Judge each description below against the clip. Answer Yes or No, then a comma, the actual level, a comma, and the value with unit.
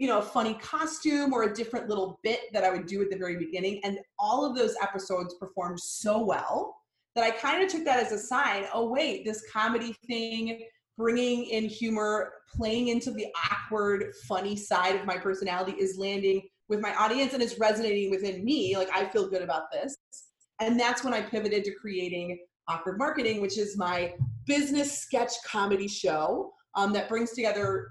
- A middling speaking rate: Yes, average, 190 wpm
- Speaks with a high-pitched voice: Yes, high, 215 Hz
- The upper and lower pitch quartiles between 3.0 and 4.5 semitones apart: Yes, average, 3.6 semitones